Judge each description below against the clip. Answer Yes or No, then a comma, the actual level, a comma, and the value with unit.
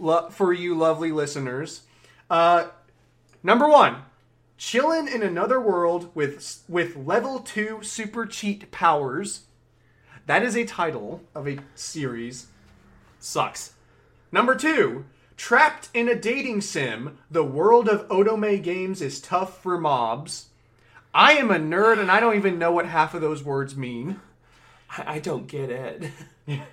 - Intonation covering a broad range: Yes, wide, 7.1 semitones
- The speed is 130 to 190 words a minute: Yes, average, 140 wpm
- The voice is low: No, medium, 170 Hz